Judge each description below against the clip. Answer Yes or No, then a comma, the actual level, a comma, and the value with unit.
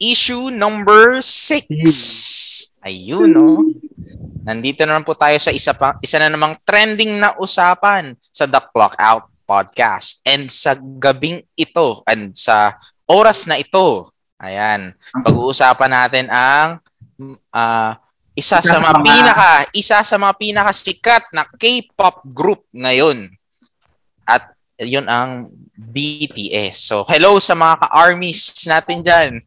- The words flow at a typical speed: Yes, average, 125 wpm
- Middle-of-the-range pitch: Yes, medium, 155 Hz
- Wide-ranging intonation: Yes, wide, 8.1 semitones